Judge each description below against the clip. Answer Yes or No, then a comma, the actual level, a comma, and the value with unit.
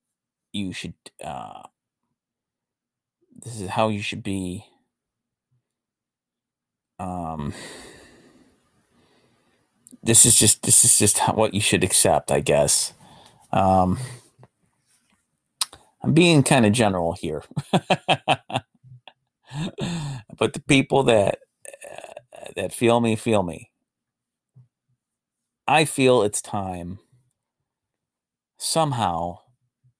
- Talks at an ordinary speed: No, slow, 90 wpm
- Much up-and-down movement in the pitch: No, average, 4.6 semitones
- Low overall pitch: Yes, low, 115 Hz